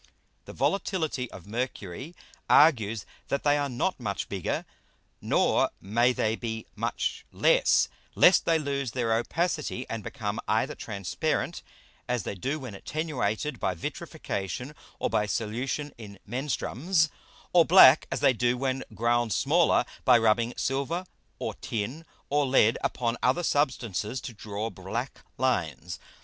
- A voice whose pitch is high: No, low, 125 Hz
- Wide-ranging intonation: No, average, 5.0 semitones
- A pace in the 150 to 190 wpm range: No, slow, 135 wpm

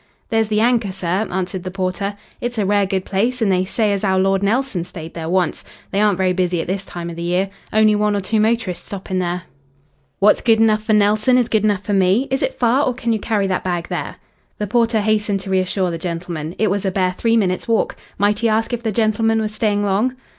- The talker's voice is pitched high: Yes, high, 205 Hz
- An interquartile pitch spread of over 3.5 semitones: No, average, 3.0 semitones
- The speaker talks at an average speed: No, fast, 240 wpm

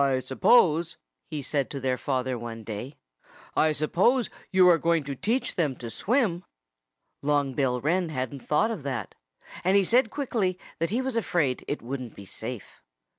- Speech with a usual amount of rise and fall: No, wide, 6.2 semitones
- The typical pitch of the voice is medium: Yes, medium, 150 Hz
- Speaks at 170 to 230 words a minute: Yes, average, 175 wpm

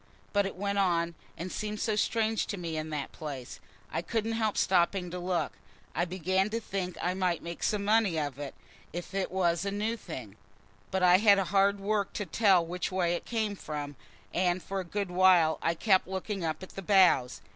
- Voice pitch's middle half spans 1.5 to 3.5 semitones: Yes, average, 2.9 semitones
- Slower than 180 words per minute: No, fast, 205 wpm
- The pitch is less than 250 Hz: Yes, medium, 185 Hz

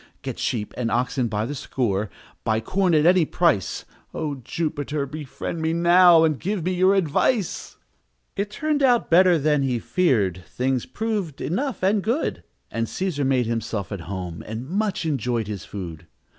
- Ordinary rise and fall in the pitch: No, wide, 8.1 semitones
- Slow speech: No, average, 165 wpm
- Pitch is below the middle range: No, medium, 150 Hz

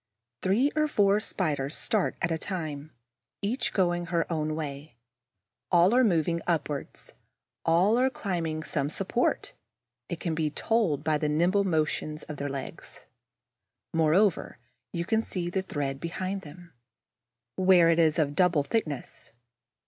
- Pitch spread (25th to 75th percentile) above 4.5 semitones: No, average, 3.8 semitones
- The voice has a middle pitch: Yes, medium, 170 Hz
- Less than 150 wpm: Yes, average, 140 wpm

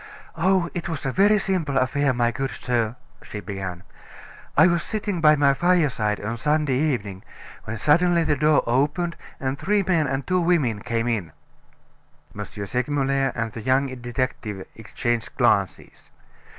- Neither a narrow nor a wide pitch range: No, wide, 6.1 semitones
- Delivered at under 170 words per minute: Yes, average, 150 wpm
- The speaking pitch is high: No, low, 135 Hz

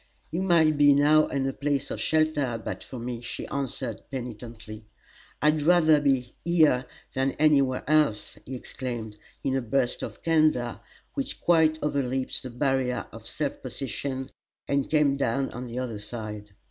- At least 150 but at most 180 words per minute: Yes, average, 160 wpm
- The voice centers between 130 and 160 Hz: Yes, low, 135 Hz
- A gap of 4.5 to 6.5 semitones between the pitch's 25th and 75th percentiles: No, average, 3.6 semitones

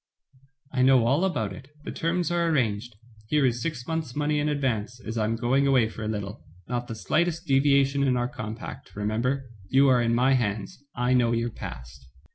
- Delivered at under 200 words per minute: No, fast, 205 wpm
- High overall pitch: No, low, 125 Hz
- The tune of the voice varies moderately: Yes, average, 3.6 semitones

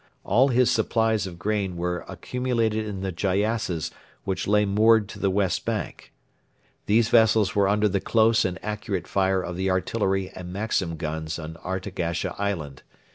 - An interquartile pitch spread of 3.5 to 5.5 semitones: No, average, 3.1 semitones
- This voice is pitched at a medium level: No, low, 100 Hz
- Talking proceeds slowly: No, average, 160 wpm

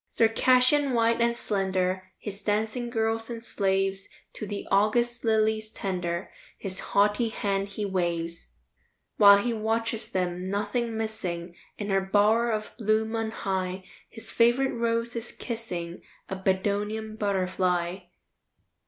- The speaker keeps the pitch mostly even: No, average, 3.0 semitones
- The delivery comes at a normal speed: No, slow, 125 wpm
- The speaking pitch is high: Yes, high, 210 Hz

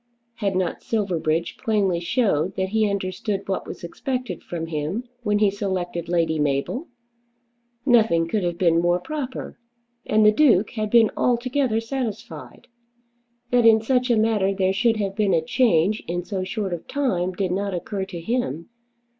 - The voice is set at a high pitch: Yes, high, 195 Hz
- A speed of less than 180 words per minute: Yes, average, 165 wpm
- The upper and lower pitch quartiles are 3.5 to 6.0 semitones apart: Yes, average, 4.4 semitones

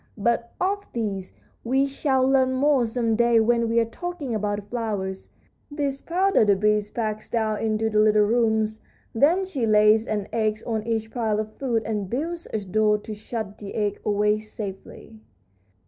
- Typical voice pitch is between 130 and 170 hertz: No, high, 220 Hz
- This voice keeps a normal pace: Yes, average, 175 wpm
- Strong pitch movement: No, average, 2.8 semitones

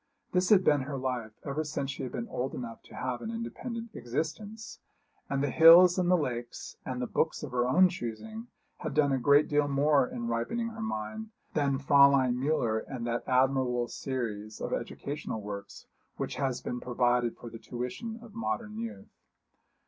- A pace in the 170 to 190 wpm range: Yes, average, 180 wpm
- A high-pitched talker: No, low, 135 Hz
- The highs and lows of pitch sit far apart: Yes, wide, 6.3 semitones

